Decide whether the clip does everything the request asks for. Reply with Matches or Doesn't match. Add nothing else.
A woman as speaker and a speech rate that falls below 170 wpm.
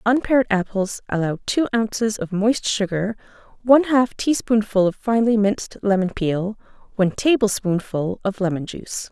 Matches